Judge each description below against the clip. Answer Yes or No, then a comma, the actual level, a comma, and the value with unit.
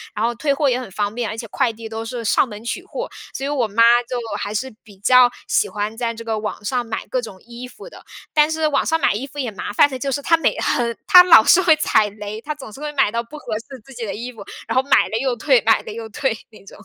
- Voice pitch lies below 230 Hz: No, high, 240 Hz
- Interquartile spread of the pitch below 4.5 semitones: Yes, average, 3.9 semitones